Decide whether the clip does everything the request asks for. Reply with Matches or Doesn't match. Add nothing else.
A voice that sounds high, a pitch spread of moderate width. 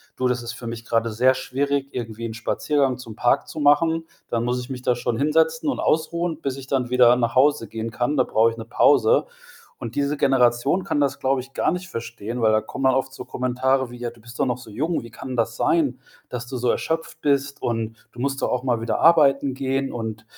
Doesn't match